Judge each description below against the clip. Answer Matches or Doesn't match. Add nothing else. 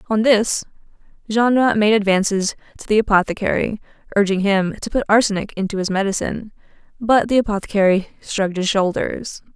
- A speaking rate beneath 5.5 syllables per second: Doesn't match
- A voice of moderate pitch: Doesn't match